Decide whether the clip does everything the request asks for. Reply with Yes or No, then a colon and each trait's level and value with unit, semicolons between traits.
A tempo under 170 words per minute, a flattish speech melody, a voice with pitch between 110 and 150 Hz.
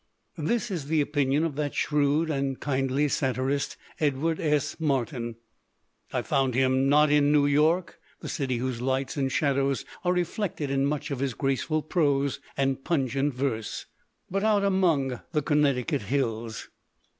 Yes: average, 155 wpm; narrow, 2.3 semitones; medium, 140 Hz